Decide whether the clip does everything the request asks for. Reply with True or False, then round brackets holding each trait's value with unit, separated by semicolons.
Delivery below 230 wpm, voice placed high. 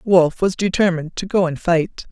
False (200 wpm; 180 Hz)